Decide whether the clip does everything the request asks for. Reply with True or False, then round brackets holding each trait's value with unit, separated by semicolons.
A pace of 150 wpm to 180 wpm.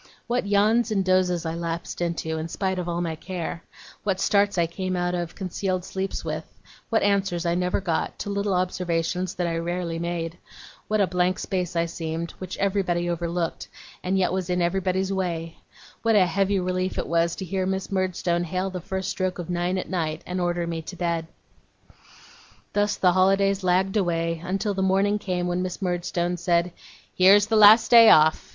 False (190 wpm)